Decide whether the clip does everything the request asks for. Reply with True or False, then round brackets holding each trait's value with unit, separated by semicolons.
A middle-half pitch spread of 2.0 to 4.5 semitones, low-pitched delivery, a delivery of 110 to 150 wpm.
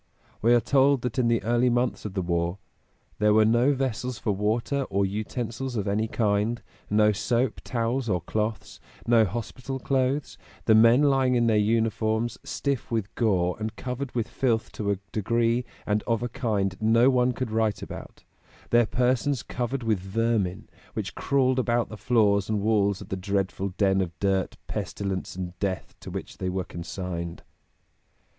False (3.3 semitones; 110 Hz; 170 wpm)